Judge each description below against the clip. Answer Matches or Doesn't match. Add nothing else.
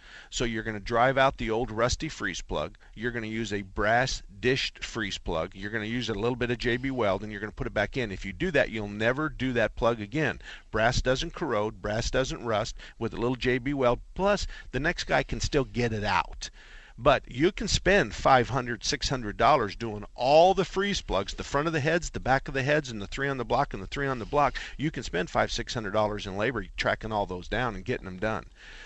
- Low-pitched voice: Matches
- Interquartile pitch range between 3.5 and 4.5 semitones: Matches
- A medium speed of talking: Doesn't match